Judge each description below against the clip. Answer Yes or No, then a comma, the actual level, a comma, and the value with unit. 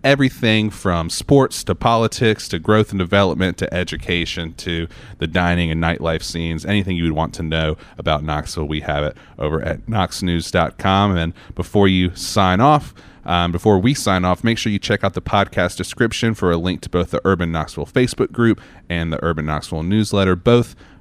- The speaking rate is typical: Yes, average, 185 wpm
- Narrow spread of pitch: No, average, 3.8 semitones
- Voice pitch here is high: No, very low, 90 Hz